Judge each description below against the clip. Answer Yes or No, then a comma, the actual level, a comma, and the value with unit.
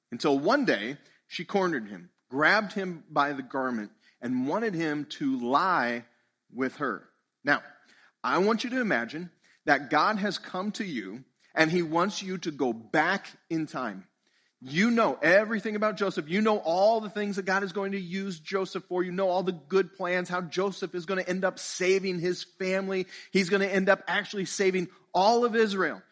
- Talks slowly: No, average, 190 wpm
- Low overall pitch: No, medium, 185 Hz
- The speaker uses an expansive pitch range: No, average, 3.5 semitones